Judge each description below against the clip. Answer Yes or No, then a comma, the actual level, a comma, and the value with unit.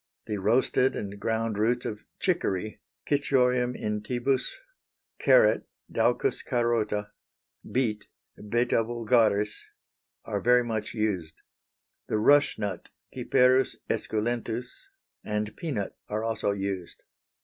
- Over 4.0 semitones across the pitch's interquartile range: No, average, 2.8 semitones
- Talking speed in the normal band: No, slow, 100 wpm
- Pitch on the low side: Yes, low, 115 Hz